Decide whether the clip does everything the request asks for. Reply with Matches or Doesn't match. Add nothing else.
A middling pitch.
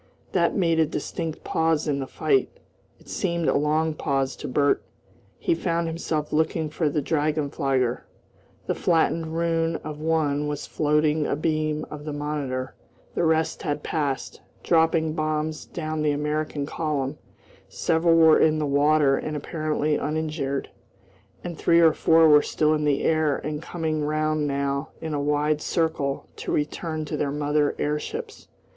Matches